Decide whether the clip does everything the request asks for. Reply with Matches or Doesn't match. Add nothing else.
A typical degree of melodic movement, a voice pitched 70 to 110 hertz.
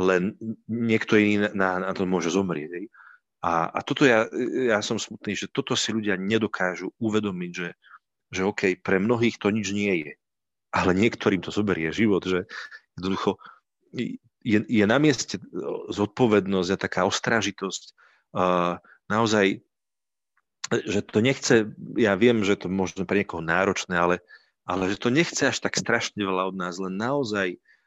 Matches